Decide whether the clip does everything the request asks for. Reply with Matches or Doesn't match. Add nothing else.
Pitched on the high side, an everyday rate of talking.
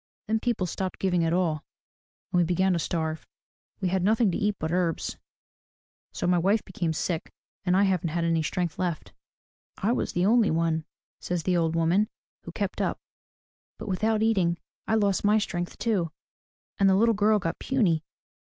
Doesn't match